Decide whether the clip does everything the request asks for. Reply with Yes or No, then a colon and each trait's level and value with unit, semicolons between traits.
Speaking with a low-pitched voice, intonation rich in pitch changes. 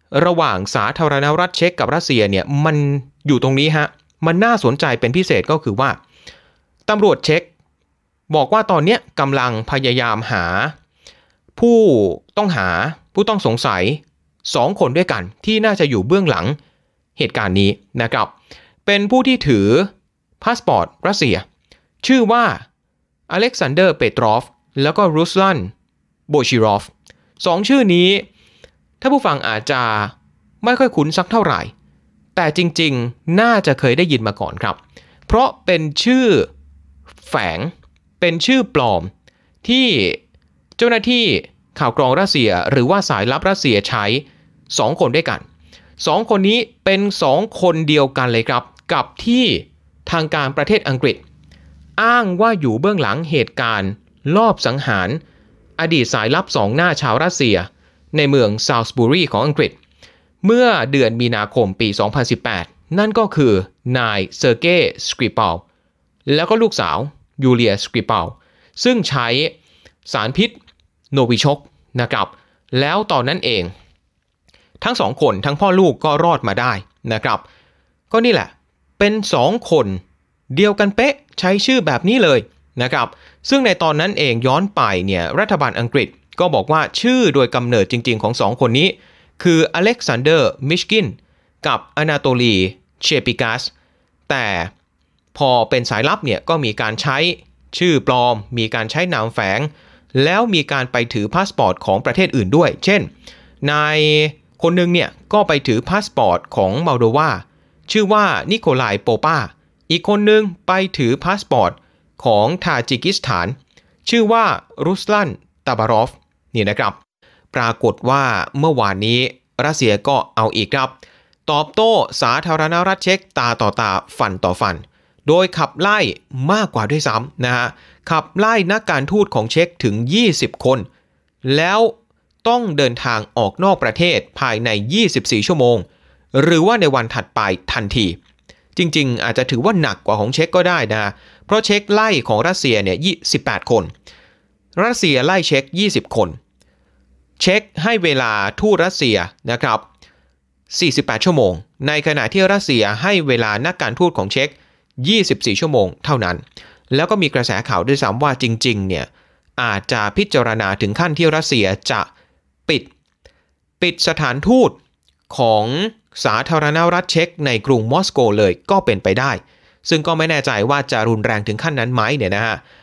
No: medium, 145 Hz; wide, 8.5 semitones